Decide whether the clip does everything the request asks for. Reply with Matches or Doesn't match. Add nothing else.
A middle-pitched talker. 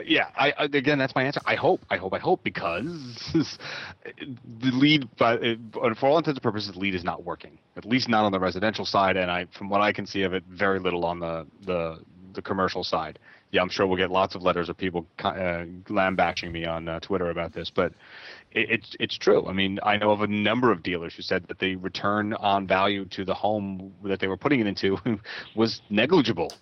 Doesn't match